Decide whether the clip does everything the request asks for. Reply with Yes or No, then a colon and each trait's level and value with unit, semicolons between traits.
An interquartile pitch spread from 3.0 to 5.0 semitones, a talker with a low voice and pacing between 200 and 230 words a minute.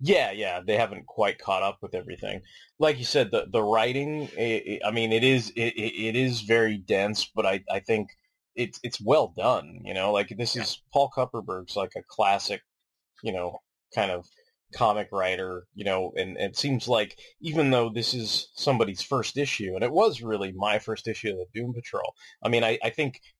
Yes: average, 3.5 semitones; low, 115 Hz; fast, 205 wpm